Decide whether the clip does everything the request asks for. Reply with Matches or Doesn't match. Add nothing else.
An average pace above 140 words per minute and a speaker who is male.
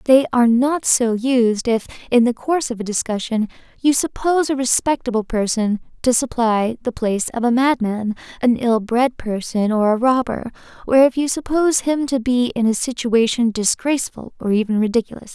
Doesn't match